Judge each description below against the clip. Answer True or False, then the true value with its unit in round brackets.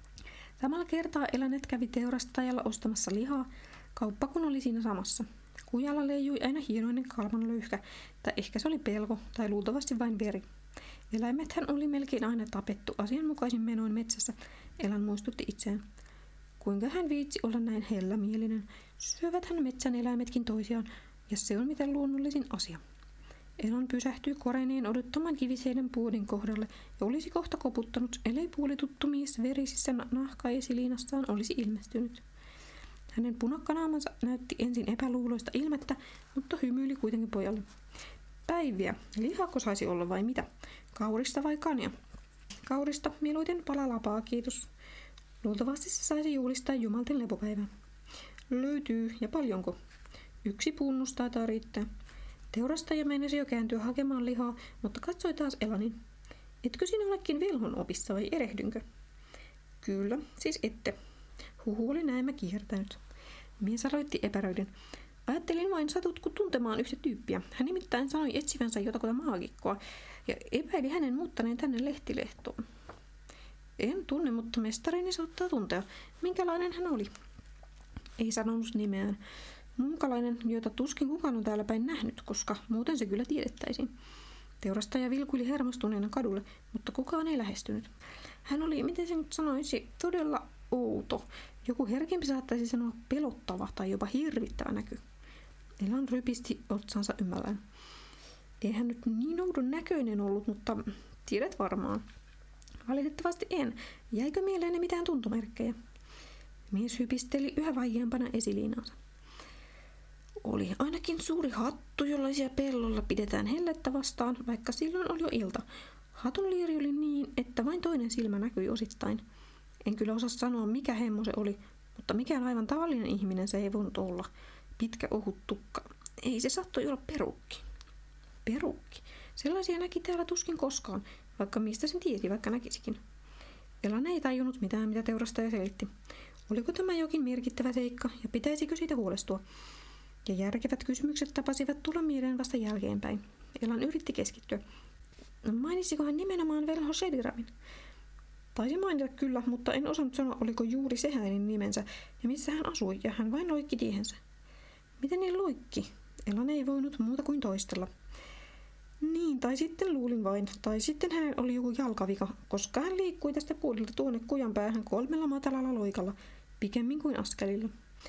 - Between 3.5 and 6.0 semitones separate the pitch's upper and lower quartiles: True (4.5 semitones)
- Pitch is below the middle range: False (250 Hz)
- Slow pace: False (135 wpm)